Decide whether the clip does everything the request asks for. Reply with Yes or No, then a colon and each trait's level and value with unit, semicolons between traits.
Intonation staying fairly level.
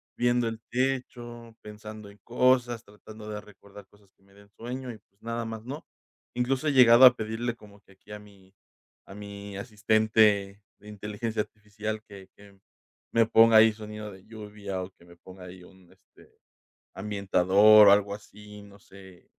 Yes: narrow, 2.3 semitones